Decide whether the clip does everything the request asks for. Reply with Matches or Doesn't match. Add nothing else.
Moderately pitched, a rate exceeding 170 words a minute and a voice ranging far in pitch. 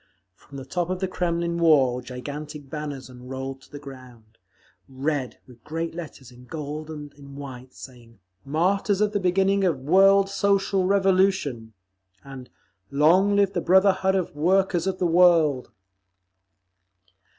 Doesn't match